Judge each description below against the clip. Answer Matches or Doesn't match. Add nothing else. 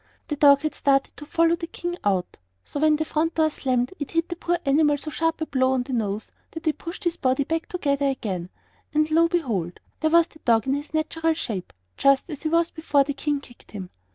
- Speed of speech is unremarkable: Doesn't match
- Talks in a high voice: Matches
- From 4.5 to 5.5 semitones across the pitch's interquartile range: Doesn't match